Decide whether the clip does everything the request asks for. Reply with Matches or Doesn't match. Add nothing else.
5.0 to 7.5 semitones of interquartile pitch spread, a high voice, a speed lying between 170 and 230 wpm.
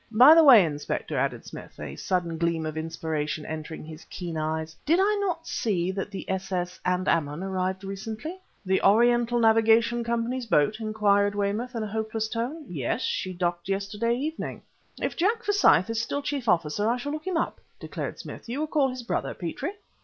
Matches